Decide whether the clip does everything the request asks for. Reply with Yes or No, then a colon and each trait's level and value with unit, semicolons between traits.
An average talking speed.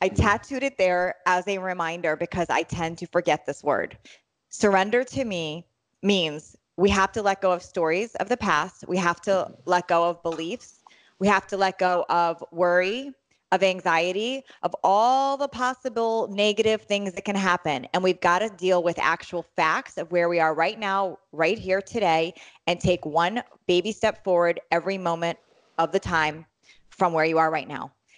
Yes: average, 185 wpm